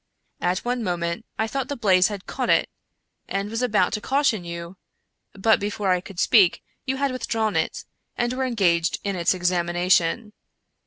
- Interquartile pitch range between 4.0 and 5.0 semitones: Yes, average, 4.6 semitones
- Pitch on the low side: No, high, 200 Hz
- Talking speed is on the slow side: No, average, 170 wpm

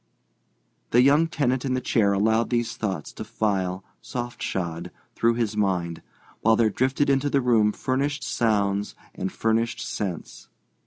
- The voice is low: Yes, low, 115 Hz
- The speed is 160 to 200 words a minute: No, average, 150 wpm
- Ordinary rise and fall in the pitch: Yes, average, 4.2 semitones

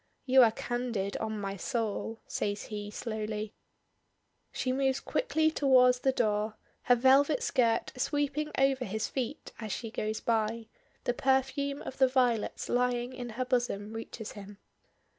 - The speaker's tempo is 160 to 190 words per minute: No, average, 145 wpm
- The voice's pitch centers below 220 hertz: No, high, 245 Hz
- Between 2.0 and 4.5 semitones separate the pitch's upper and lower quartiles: Yes, average, 3.4 semitones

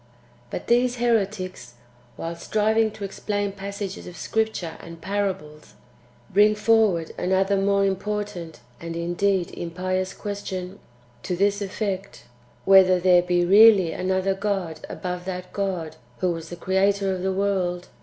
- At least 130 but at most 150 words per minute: Yes, average, 140 wpm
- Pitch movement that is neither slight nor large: No, narrow, 2.2 semitones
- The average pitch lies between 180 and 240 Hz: Yes, high, 190 Hz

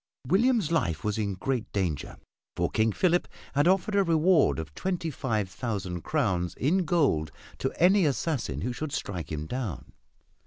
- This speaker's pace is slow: No, average, 160 wpm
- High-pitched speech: No, low, 130 Hz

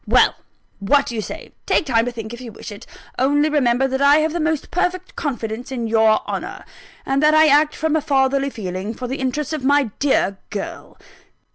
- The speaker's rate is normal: No, fast, 210 wpm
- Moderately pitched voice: No, very high, 265 Hz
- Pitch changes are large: No, average, 4.5 semitones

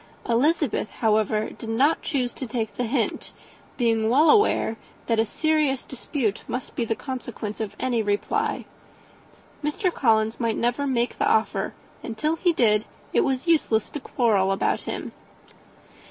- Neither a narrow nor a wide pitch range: Yes, average, 4.2 semitones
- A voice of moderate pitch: No, high, 240 Hz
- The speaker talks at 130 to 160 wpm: Yes, average, 155 wpm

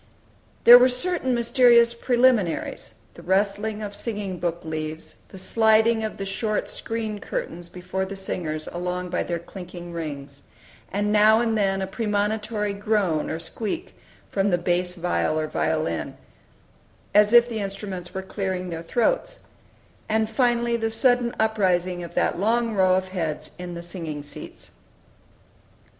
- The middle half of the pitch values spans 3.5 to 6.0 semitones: Yes, average, 4.1 semitones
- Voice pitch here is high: Yes, high, 200 Hz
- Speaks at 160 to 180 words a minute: No, average, 145 wpm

